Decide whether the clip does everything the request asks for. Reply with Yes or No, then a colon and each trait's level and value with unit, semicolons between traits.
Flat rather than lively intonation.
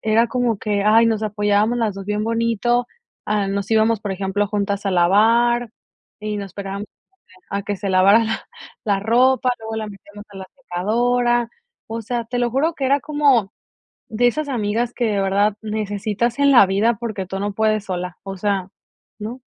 No: average, 3.0 semitones